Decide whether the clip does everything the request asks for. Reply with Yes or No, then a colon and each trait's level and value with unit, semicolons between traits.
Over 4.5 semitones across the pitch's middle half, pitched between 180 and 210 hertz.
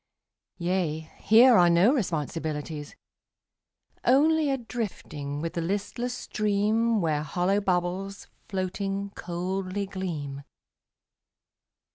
No: average, 4.2 semitones; high, 190 Hz